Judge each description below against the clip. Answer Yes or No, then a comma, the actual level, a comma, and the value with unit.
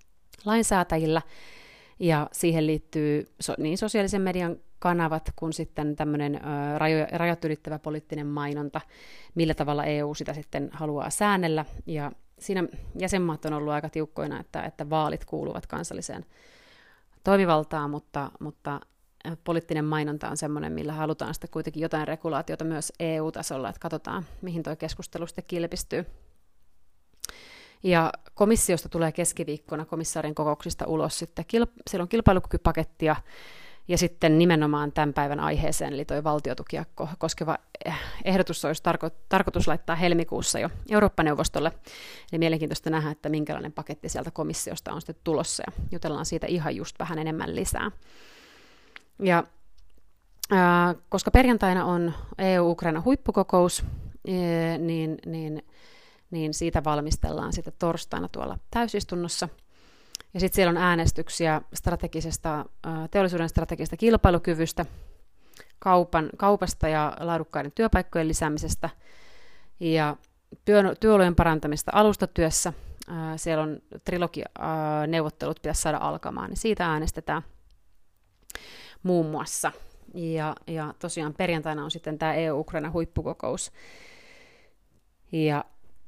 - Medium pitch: Yes, medium, 160 Hz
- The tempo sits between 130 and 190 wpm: No, average, 110 wpm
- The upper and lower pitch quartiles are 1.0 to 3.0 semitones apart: Yes, narrow, 2.6 semitones